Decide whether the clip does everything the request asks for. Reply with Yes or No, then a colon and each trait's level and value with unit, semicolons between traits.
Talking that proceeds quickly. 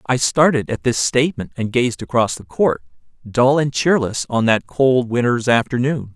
No: average, 165 wpm